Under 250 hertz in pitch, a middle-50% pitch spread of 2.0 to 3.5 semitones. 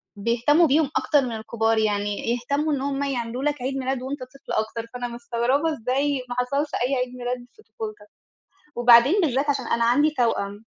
No: very high, 255 Hz; average, 3.2 semitones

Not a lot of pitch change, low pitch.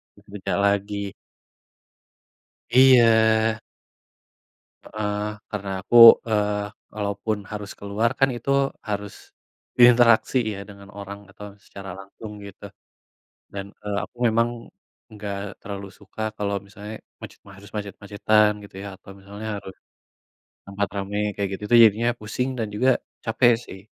Yes: narrow, 1.7 semitones; low, 105 Hz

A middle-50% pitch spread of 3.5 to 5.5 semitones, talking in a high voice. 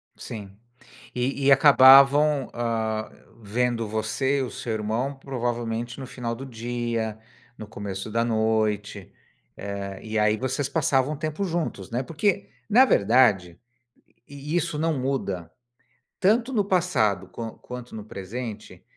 No: average, 4.2 semitones; low, 120 Hz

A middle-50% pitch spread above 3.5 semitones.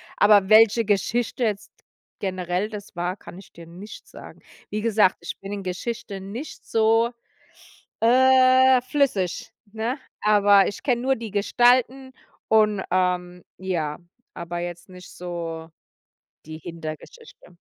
Yes: average, 4.5 semitones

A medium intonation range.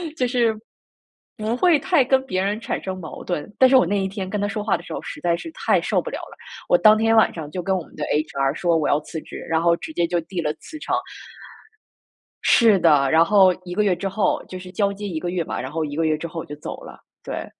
Yes: average, 4.7 semitones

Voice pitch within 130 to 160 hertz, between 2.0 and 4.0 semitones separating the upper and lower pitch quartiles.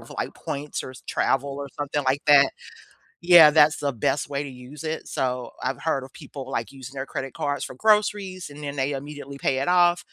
Yes: medium, 140 Hz; narrow, 2.5 semitones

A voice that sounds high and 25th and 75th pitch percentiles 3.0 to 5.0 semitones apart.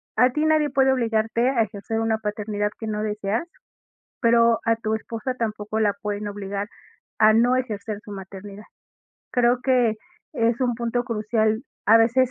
No: high, 225 Hz; narrow, 2.5 semitones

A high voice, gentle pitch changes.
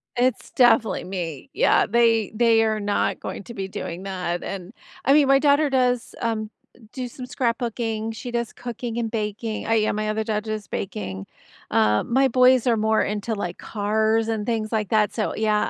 Yes: high, 220 Hz; narrow, 2.3 semitones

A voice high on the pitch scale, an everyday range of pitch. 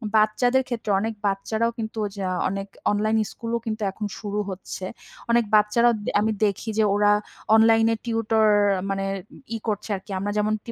No: high, 215 Hz; narrow, 1.8 semitones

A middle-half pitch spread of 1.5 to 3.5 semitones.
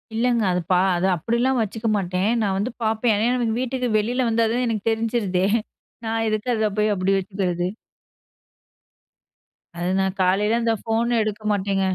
Yes: average, 3.2 semitones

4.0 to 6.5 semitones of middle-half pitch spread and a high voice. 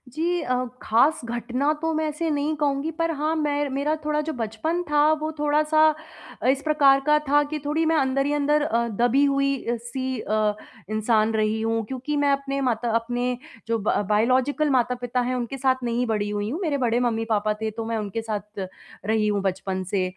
Yes: average, 4.7 semitones; very high, 255 Hz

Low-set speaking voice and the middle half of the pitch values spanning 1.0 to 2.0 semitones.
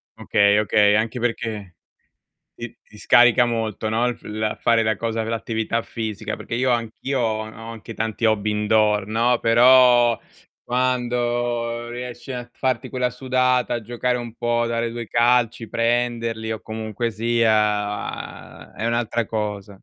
Yes: low, 115 Hz; narrow, 1.7 semitones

